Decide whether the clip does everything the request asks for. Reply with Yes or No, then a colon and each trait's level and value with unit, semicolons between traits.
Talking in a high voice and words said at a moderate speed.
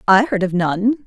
No: high, 210 Hz; fast, 225 wpm